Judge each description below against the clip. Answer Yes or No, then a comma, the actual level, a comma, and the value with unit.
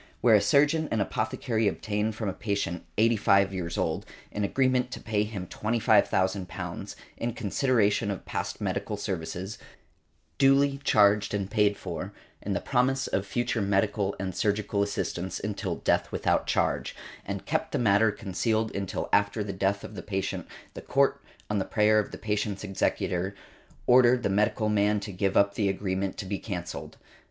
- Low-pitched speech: Yes, low, 105 Hz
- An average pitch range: No, narrow, 2.2 semitones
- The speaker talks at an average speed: Yes, average, 165 wpm